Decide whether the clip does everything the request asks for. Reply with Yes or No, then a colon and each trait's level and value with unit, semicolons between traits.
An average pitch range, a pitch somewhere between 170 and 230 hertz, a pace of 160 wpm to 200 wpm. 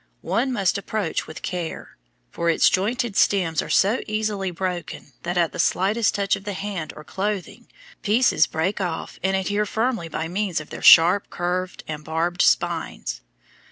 Yes: average, 3.5 semitones; high, 190 Hz; average, 165 wpm